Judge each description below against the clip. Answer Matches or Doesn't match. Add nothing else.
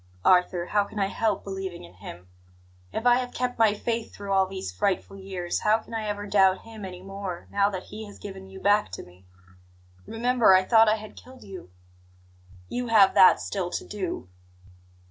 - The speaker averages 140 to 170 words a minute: Doesn't match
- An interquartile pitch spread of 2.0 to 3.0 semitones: Matches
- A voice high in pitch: Matches